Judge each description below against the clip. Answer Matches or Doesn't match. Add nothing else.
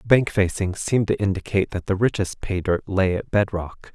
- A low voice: Matches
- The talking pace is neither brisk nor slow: Doesn't match